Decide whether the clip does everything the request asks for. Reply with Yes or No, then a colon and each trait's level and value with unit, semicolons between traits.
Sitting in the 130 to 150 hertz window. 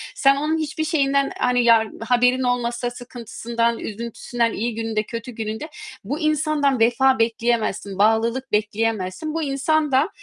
No: high, 245 Hz